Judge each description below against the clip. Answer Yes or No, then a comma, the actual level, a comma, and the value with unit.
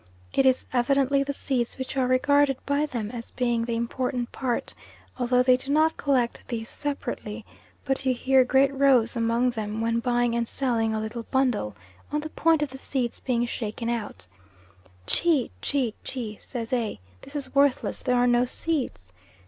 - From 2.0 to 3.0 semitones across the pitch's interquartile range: Yes, average, 2.7 semitones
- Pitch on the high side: Yes, very high, 250 Hz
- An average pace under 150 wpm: No, average, 175 wpm